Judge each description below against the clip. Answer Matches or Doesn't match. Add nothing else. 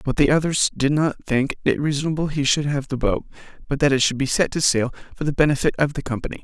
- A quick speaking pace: Matches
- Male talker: Matches